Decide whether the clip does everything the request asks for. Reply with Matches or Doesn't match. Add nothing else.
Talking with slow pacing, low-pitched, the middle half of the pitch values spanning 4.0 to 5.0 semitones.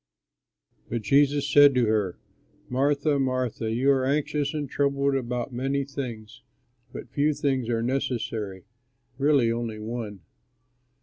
Doesn't match